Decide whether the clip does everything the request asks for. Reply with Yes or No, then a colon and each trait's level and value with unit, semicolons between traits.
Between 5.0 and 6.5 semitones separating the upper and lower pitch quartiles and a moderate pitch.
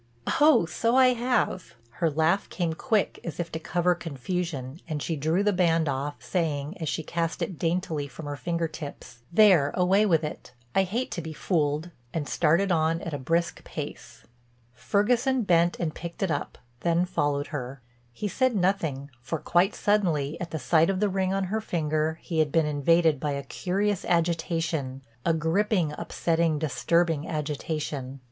No: average, 3.4 semitones; medium, 165 Hz